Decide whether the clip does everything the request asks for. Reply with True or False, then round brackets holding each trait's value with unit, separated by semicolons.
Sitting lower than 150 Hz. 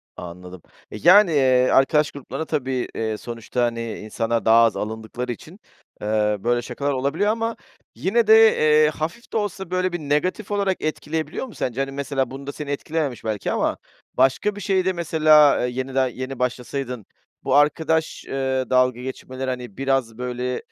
True (135 Hz)